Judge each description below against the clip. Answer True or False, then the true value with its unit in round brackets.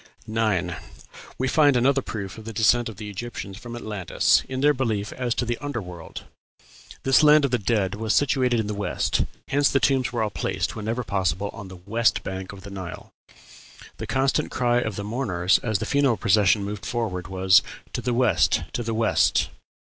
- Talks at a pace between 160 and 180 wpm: False (195 wpm)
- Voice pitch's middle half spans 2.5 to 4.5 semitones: True (3.8 semitones)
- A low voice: True (110 Hz)